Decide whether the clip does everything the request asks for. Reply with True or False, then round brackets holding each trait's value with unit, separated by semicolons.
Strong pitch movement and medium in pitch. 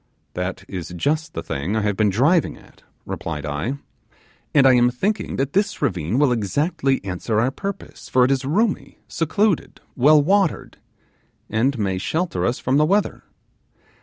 False (7.6 semitones; 130 Hz)